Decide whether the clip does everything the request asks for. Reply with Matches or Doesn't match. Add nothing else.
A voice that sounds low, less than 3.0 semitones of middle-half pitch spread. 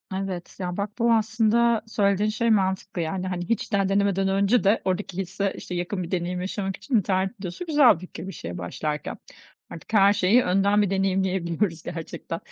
Doesn't match